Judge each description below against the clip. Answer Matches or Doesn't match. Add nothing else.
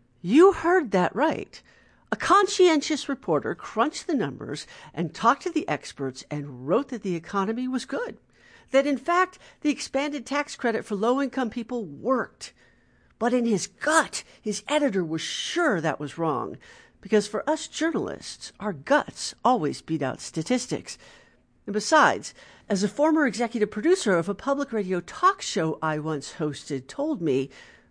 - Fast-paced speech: Doesn't match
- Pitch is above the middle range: Matches